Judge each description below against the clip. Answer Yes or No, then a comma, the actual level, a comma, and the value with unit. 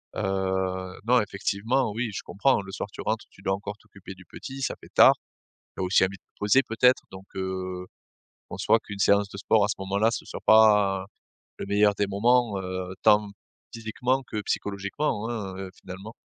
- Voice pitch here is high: No, low, 100 Hz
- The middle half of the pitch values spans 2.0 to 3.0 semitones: Yes, narrow, 2.5 semitones